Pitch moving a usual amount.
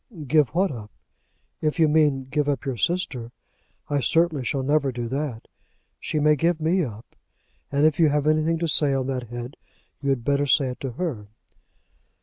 Yes: average, 3.2 semitones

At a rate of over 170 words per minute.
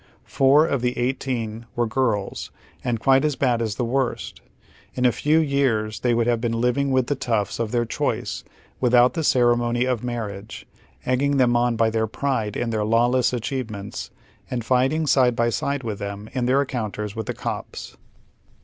Yes: average, 190 wpm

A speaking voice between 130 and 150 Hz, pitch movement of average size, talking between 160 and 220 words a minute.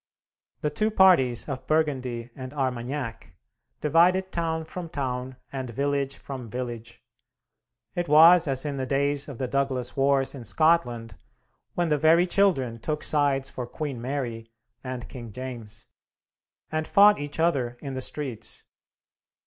No: low, 135 Hz; average, 3.9 semitones; average, 140 wpm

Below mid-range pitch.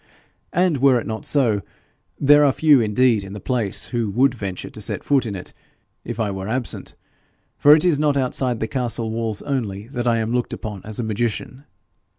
Yes: low, 120 Hz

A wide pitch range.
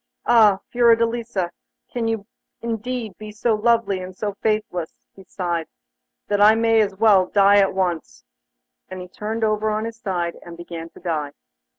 No: average, 3.6 semitones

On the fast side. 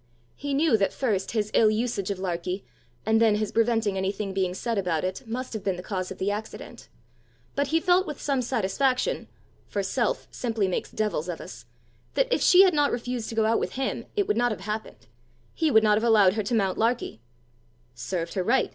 Yes: fast, 215 wpm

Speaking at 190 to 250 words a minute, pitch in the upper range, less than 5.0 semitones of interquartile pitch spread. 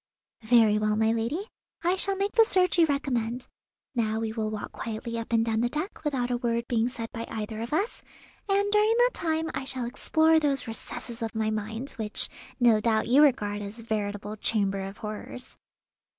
No: average, 195 wpm; high, 235 Hz; wide, 5.4 semitones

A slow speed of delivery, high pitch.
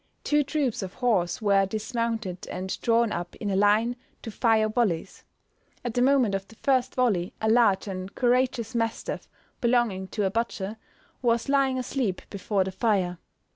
No: average, 165 wpm; high, 225 Hz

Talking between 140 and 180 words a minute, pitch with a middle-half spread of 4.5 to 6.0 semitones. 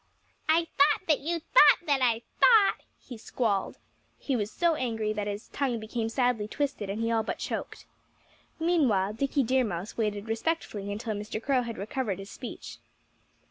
Yes: average, 175 wpm; average, 5.0 semitones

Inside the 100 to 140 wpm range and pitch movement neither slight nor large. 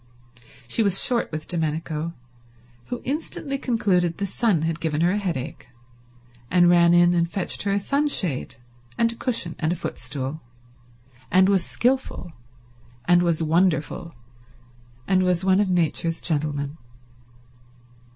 Yes: slow, 135 wpm; average, 3.6 semitones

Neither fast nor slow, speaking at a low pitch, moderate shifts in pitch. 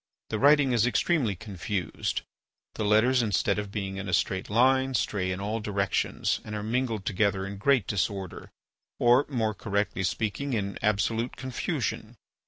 Yes: average, 155 wpm; low, 105 Hz; average, 3.7 semitones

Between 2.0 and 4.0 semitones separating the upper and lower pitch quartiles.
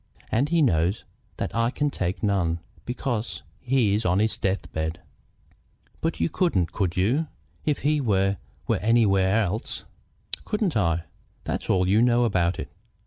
No: average, 5.1 semitones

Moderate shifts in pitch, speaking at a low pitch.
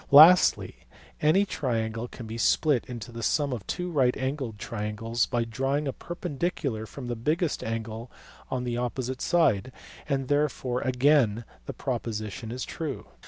Yes: average, 4.1 semitones; low, 125 Hz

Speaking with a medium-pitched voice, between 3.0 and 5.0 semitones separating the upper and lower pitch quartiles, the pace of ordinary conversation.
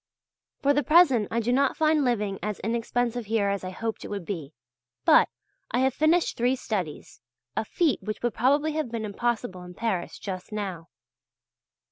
No: high, 230 Hz; average, 4.6 semitones; average, 175 wpm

